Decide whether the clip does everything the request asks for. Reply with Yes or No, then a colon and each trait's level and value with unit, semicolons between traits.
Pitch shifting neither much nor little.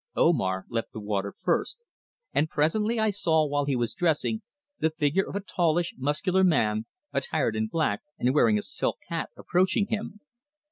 No: wide, 8.2 semitones